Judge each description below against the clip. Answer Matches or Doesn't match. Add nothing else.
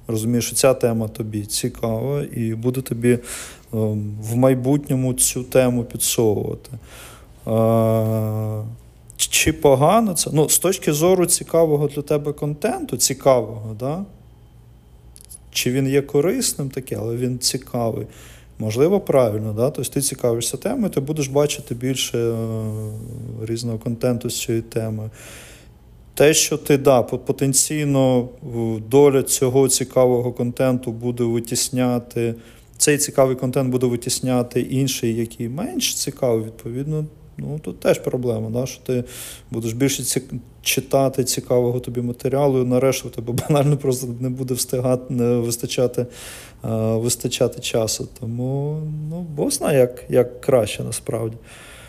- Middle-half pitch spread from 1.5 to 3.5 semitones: Matches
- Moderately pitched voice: Doesn't match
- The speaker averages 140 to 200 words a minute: Doesn't match